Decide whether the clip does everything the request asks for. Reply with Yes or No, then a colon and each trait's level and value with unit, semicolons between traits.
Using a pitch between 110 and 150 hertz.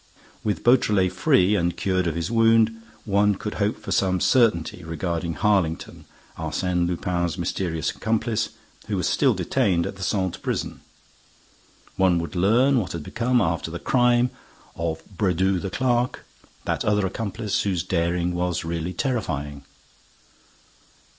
No: very low, 95 Hz